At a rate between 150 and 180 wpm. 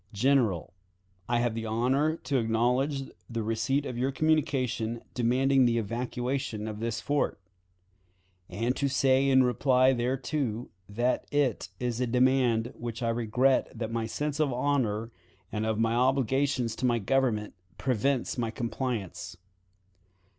No: average, 140 wpm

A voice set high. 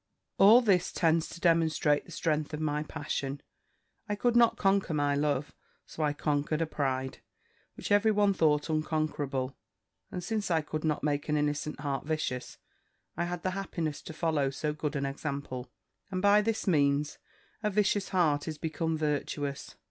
No: medium, 155 Hz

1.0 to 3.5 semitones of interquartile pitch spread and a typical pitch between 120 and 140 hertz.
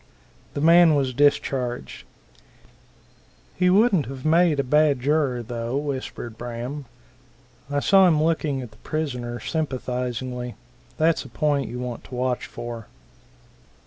No: average, 3.9 semitones; low, 135 Hz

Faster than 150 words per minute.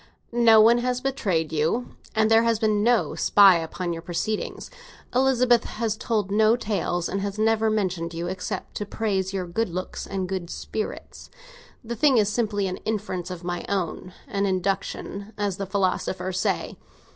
Yes: average, 165 wpm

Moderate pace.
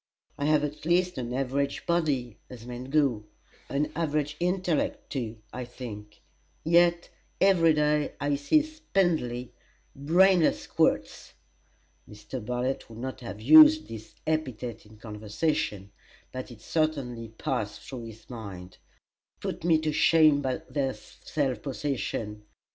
No: slow, 130 wpm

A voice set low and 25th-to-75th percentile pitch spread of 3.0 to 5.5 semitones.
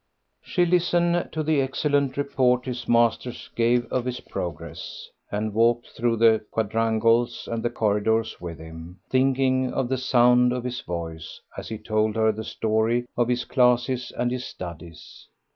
No: low, 120 Hz; narrow, 2.6 semitones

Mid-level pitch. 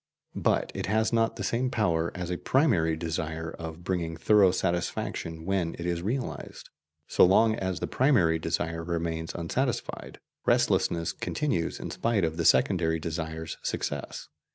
No: very low, 85 Hz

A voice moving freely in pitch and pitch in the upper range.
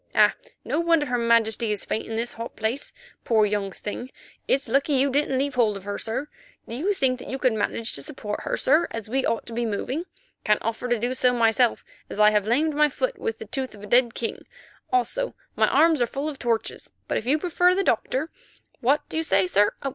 No: average, 4.6 semitones; high, 245 Hz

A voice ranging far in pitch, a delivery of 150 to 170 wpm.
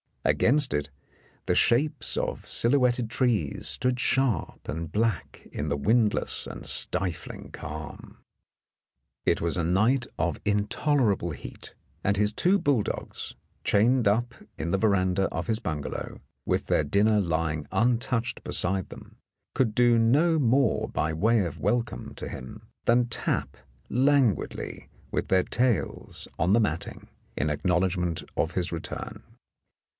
No: wide, 6.0 semitones; average, 140 wpm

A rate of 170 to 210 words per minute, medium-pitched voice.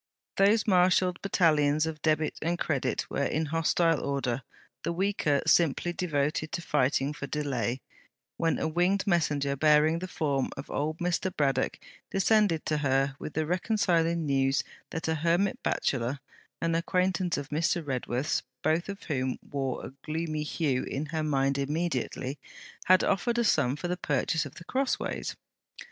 No: average, 155 wpm; medium, 155 Hz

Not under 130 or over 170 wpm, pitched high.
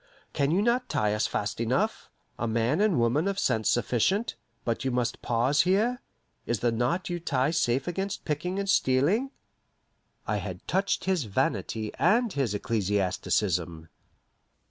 No: average, 150 wpm; low, 135 Hz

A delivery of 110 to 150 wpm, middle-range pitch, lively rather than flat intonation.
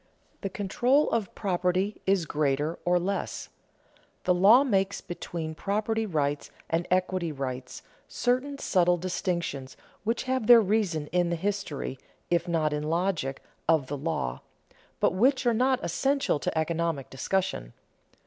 No: average, 140 wpm; medium, 180 Hz; average, 4.7 semitones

